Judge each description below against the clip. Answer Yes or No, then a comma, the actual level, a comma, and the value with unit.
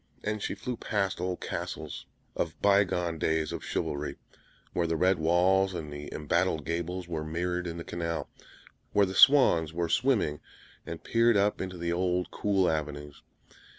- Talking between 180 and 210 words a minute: No, average, 165 wpm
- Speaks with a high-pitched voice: No, very low, 85 Hz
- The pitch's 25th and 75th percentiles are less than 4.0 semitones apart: Yes, average, 3.0 semitones